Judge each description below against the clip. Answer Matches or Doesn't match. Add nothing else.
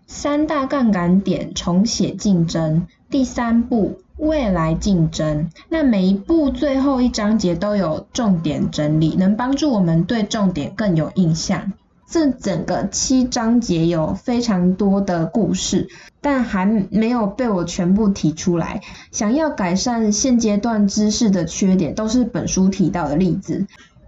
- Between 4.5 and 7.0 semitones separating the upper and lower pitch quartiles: Matches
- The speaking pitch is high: Matches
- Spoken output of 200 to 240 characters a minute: Matches